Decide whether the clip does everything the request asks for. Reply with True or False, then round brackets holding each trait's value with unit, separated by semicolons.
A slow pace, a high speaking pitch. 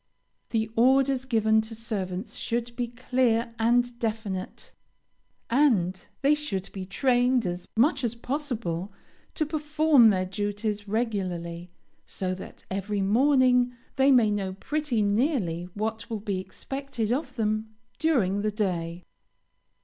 True (125 wpm; 225 Hz)